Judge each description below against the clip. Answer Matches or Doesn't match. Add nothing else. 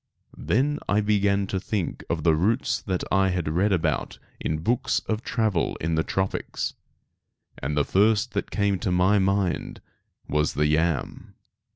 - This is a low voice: Matches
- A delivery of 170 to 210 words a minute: Doesn't match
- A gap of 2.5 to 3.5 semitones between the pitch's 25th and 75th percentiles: Doesn't match